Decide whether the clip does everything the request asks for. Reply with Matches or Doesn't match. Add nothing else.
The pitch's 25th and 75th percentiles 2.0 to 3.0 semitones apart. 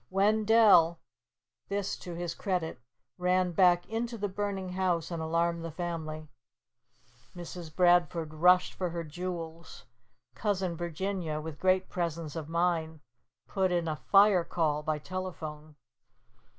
Matches